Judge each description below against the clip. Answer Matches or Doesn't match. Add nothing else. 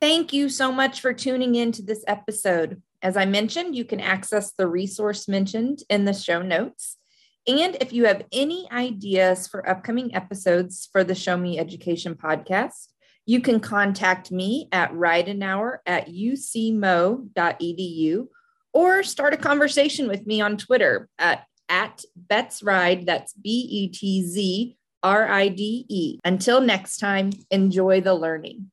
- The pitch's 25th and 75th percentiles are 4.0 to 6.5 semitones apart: Matches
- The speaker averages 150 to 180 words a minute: Doesn't match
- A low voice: Doesn't match